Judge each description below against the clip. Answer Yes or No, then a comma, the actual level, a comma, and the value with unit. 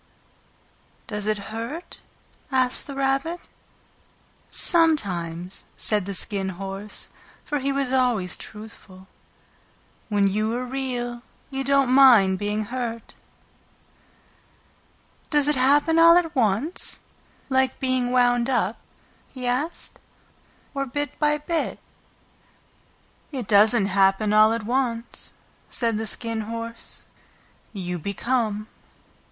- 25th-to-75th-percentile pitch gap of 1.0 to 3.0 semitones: No, average, 4.5 semitones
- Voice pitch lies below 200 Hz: No, high, 235 Hz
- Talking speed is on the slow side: Yes, slow, 110 wpm